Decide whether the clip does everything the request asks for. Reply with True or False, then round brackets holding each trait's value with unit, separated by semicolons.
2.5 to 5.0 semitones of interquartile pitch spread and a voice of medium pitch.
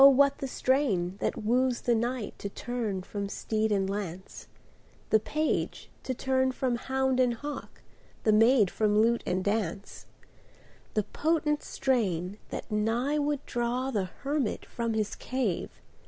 False (4.1 semitones; 235 Hz)